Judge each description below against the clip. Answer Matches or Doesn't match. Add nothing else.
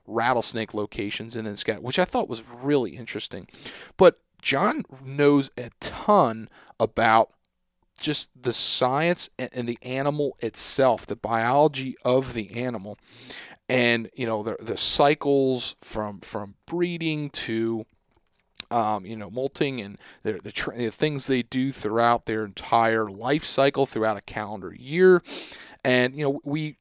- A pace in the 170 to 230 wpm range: Doesn't match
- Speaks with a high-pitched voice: Doesn't match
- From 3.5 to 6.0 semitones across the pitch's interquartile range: Matches